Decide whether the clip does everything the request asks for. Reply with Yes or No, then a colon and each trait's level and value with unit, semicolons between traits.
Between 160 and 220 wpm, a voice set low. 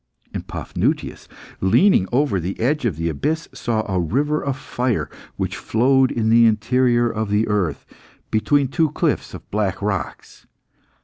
No: average, 150 wpm; low, 115 Hz